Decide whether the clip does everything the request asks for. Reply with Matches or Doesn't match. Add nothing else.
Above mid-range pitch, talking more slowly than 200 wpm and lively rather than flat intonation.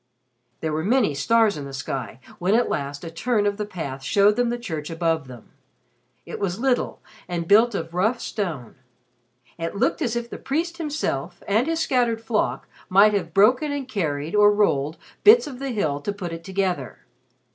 Matches